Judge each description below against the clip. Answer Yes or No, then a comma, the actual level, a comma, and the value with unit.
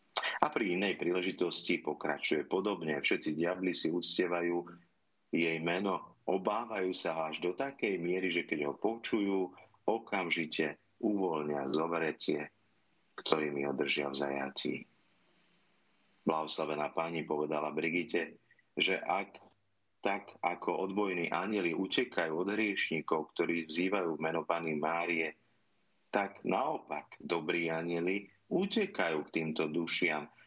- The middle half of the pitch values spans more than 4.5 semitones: No, average, 2.9 semitones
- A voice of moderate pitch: No, very low, 85 Hz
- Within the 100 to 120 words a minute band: Yes, slow, 110 wpm